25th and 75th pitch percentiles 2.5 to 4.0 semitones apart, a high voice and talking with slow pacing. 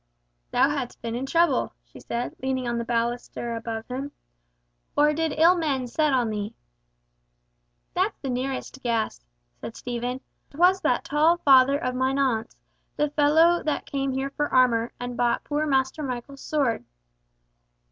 No: average, 3.6 semitones; very high, 265 Hz; average, 155 wpm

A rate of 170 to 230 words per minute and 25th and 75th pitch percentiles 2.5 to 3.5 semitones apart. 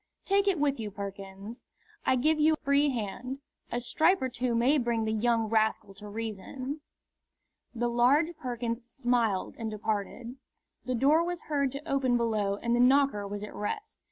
No: average, 175 wpm; average, 4.3 semitones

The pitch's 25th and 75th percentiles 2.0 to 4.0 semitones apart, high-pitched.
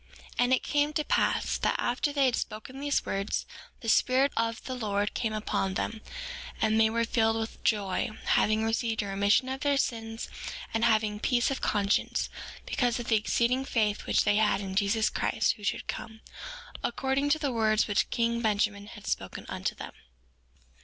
Yes: average, 3.0 semitones; high, 225 Hz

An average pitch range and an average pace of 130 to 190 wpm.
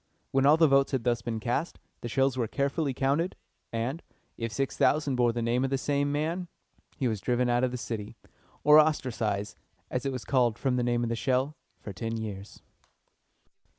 No: average, 3.1 semitones; average, 200 wpm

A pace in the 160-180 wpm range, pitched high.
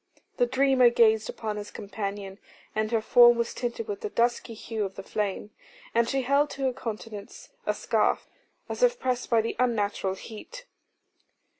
Yes: average, 170 wpm; high, 230 Hz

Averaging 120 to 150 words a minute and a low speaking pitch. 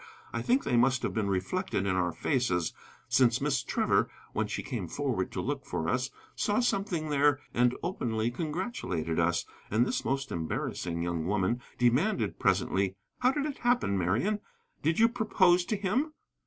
No: average, 170 wpm; low, 130 Hz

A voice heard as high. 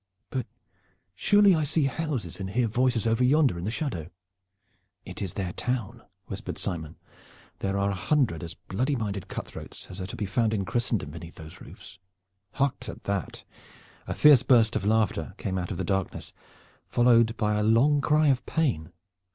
No: low, 110 Hz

